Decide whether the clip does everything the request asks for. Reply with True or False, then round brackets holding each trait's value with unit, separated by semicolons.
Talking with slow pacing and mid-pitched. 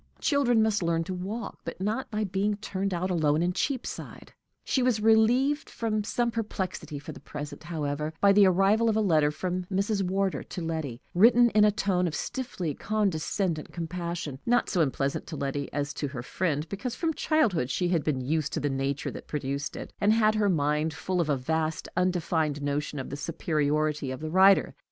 False (195 wpm; 180 Hz)